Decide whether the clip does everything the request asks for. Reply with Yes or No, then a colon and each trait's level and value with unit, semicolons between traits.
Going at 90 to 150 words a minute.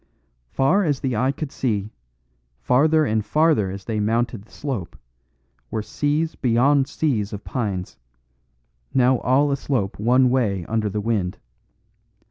Yes: slow, 135 wpm